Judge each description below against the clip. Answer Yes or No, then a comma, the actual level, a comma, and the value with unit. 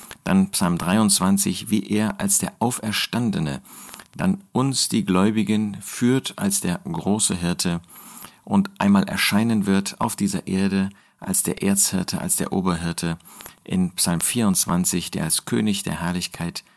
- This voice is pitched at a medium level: No, low, 110 Hz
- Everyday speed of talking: Yes, average, 135 wpm